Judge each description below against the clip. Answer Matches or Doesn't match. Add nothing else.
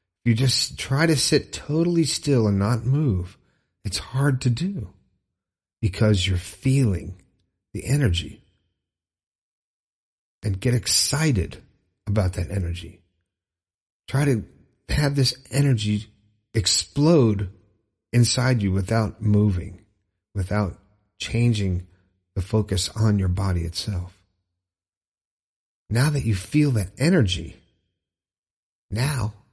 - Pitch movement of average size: Matches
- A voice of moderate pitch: Doesn't match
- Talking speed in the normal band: Doesn't match